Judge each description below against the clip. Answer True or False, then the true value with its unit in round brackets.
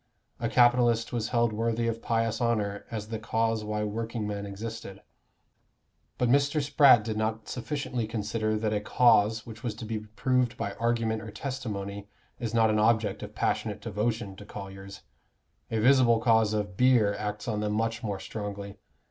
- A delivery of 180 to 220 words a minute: False (165 wpm)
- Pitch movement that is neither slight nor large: False (1.9 semitones)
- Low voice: True (110 Hz)